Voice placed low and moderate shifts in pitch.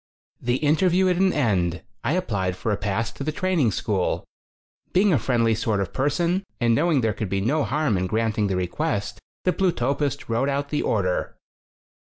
No: low, 125 Hz; wide, 7.0 semitones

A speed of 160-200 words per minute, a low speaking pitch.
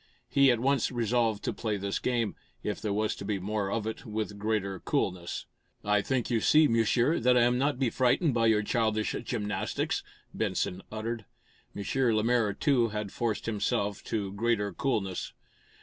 Yes: average, 170 wpm; low, 110 Hz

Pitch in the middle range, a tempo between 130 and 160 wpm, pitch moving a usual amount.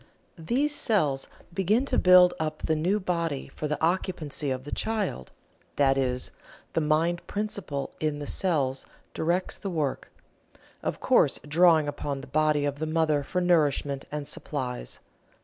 Yes: medium, 155 Hz; average, 150 wpm; average, 4.0 semitones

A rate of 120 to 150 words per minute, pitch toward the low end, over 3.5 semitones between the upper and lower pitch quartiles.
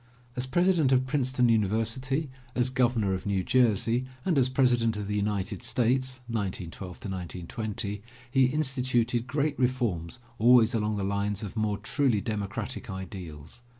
Yes: average, 140 wpm; low, 115 Hz; average, 4.2 semitones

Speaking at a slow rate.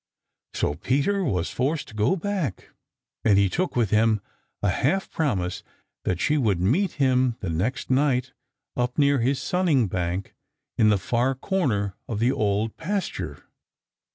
No: average, 155 wpm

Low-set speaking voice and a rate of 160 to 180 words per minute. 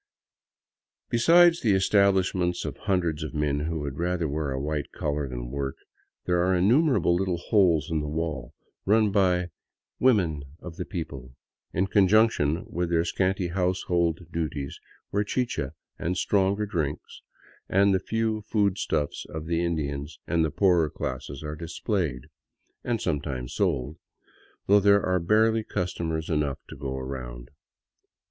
No: very low, 85 Hz; average, 150 wpm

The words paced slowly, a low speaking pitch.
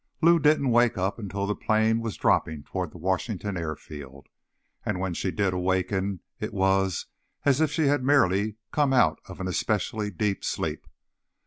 No: average, 175 wpm; low, 100 Hz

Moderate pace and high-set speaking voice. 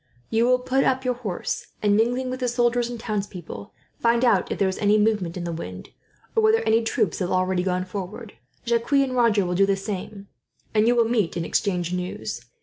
No: fast, 215 wpm; high, 215 Hz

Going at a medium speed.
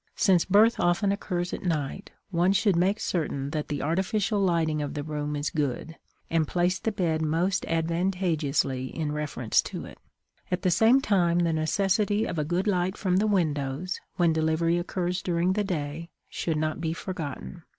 Yes: average, 175 wpm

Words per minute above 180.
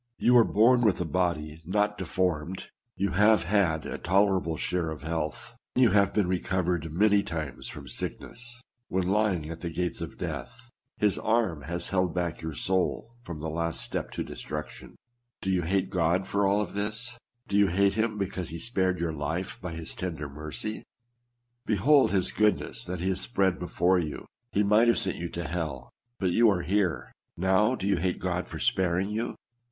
Yes: average, 190 wpm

